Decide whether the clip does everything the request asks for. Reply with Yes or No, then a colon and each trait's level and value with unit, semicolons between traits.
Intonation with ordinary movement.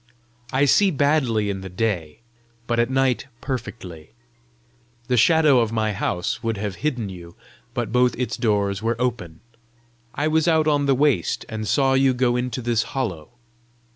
Yes: average, 4.4 semitones